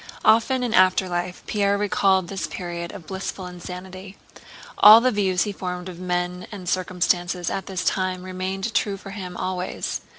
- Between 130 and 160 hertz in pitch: No, medium, 185 Hz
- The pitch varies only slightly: Yes, narrow, 1.6 semitones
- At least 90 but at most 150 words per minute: No, average, 160 wpm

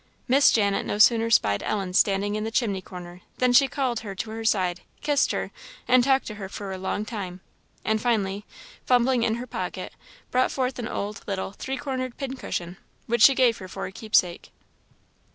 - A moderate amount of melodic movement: Yes, average, 4.5 semitones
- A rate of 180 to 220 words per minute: Yes, average, 190 wpm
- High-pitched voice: Yes, high, 220 Hz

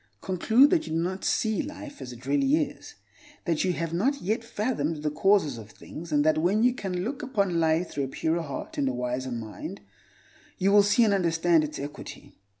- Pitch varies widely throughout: Yes, wide, 5.8 semitones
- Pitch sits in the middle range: Yes, medium, 170 Hz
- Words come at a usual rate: No, fast, 210 wpm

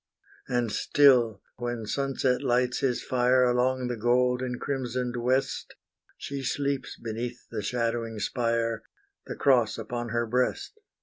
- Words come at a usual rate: No, slow, 130 wpm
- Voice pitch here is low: Yes, low, 125 Hz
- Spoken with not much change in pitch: Yes, narrow, 1.7 semitones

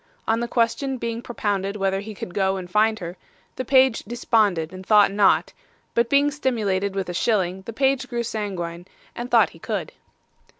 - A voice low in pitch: No, high, 210 Hz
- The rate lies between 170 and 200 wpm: Yes, average, 180 wpm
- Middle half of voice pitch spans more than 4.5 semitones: No, average, 3.7 semitones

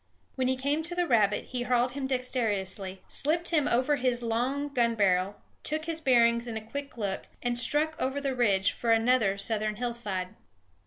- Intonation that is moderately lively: Yes, average, 4.1 semitones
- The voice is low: No, high, 245 Hz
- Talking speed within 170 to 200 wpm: Yes, average, 180 wpm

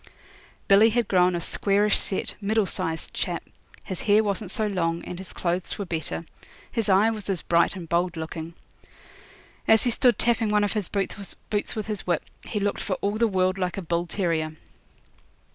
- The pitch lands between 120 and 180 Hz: No, high, 195 Hz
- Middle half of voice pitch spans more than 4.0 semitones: No, average, 3.4 semitones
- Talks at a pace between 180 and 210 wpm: Yes, average, 185 wpm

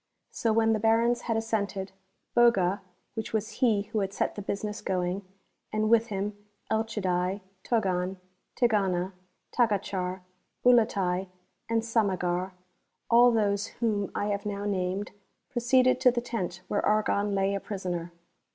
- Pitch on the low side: No, high, 205 Hz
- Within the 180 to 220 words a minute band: No, average, 140 wpm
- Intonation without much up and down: No, average, 3.0 semitones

